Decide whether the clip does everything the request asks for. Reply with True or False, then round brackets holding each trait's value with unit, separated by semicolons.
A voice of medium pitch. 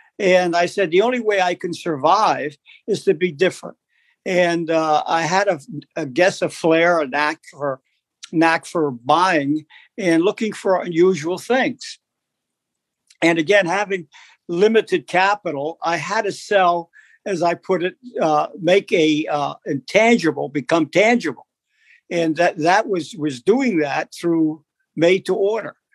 True (175 Hz)